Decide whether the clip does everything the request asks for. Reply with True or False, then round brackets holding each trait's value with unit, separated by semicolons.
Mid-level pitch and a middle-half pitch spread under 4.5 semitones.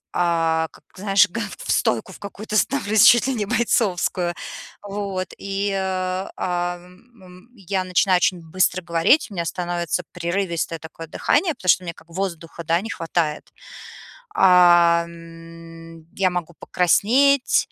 True (180 Hz; 2.7 semitones)